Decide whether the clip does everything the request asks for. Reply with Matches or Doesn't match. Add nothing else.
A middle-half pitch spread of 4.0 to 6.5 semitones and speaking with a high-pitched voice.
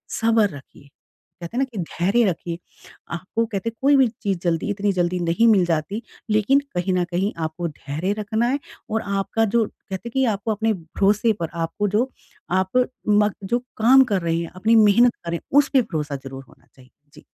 Matches